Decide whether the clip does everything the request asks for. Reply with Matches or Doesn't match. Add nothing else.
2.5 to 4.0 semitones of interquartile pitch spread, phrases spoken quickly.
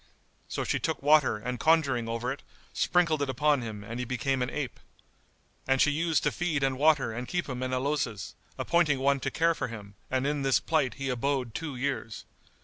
Matches